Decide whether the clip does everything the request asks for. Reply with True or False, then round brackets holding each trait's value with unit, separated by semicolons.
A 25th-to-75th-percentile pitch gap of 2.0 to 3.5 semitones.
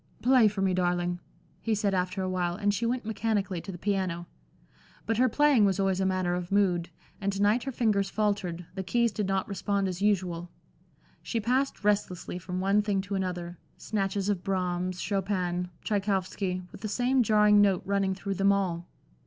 True (2.4 semitones)